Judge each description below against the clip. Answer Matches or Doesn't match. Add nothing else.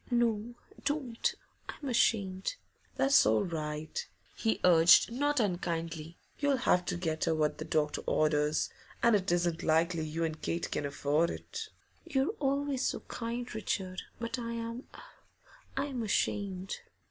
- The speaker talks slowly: Doesn't match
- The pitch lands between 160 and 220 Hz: Matches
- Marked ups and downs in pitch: Matches